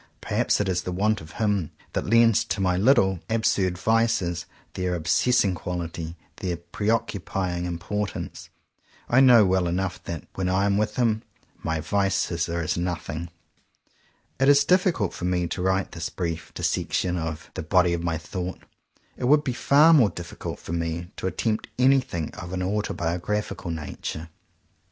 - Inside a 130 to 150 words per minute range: No, average, 160 wpm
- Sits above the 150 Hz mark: No, very low, 95 Hz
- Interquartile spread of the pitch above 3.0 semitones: Yes, average, 3.8 semitones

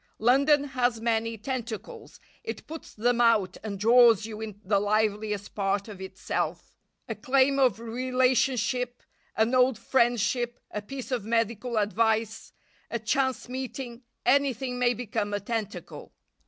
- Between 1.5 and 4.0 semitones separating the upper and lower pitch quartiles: Yes, average, 2.9 semitones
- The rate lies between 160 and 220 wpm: No, slow, 135 wpm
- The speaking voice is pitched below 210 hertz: No, high, 230 Hz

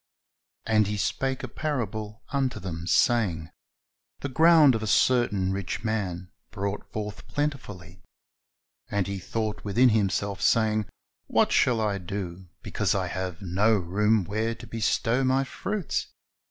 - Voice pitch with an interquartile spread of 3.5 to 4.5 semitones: Yes, average, 3.8 semitones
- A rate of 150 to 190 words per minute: No, average, 140 wpm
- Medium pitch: No, low, 105 Hz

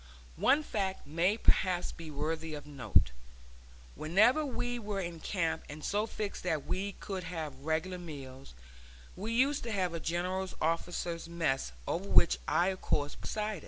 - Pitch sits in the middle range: Yes, medium, 175 Hz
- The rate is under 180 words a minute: Yes, average, 160 wpm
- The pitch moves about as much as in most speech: Yes, average, 4.1 semitones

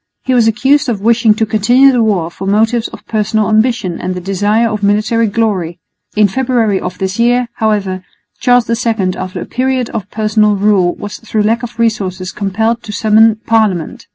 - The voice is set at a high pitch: Yes, high, 215 Hz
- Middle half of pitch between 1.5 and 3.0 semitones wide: Yes, average, 2.7 semitones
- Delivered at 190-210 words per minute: No, average, 180 wpm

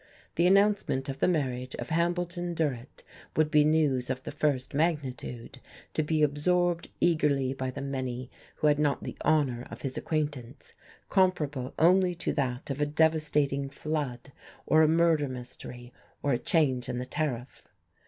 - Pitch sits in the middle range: Yes, medium, 145 Hz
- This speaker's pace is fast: No, average, 160 wpm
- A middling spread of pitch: Yes, average, 3.6 semitones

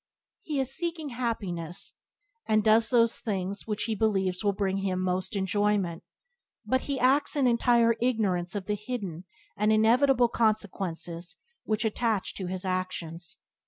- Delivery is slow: No, average, 145 wpm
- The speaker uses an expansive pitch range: No, average, 4.1 semitones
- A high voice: Yes, high, 210 Hz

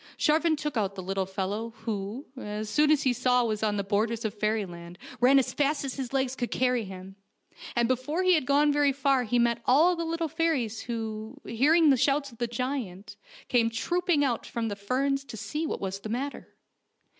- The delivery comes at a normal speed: No, fast, 210 wpm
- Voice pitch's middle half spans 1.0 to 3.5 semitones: No, average, 4.8 semitones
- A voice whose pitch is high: Yes, high, 245 Hz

